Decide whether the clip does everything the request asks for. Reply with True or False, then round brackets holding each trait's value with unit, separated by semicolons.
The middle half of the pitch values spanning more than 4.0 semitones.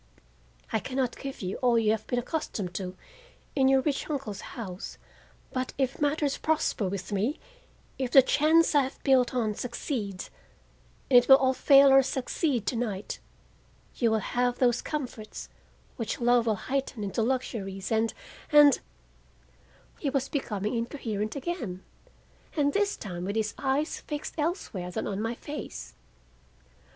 True (4.6 semitones)